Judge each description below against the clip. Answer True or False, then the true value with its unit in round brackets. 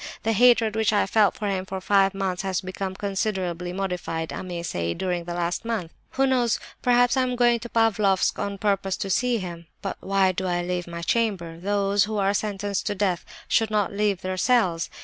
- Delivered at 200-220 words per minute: True (205 wpm)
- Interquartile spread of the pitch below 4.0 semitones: True (3.1 semitones)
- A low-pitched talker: False (195 Hz)